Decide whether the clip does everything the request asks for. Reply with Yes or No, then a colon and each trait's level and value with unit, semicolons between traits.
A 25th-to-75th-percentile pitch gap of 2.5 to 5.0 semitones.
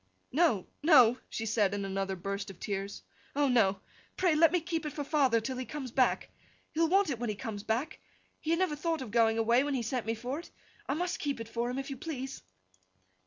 No: wide, 5.4 semitones